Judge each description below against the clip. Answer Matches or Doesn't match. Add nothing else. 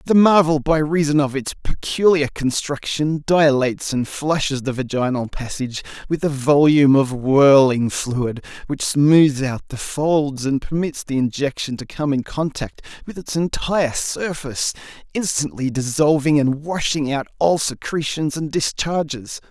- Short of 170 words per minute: Matches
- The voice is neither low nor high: Matches